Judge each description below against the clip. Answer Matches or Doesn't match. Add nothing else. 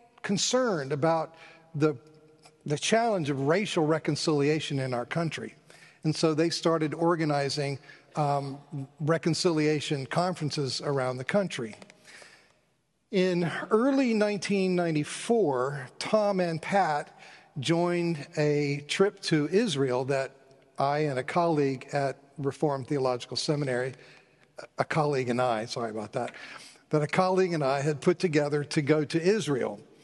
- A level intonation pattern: Doesn't match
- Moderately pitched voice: Matches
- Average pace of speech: Doesn't match